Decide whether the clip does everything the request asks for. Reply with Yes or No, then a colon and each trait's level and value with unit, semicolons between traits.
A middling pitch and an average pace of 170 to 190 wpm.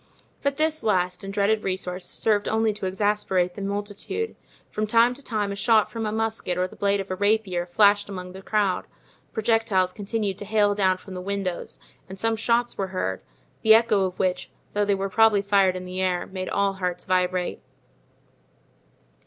No: high, 200 Hz; average, 185 wpm